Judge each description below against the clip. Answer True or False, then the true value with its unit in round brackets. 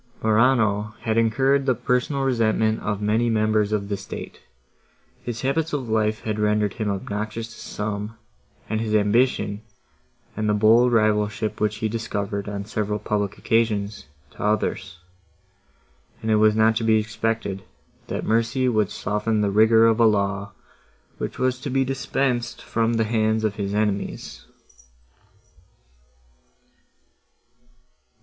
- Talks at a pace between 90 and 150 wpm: True (135 wpm)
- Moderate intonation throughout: False (1.6 semitones)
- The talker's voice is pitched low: True (110 Hz)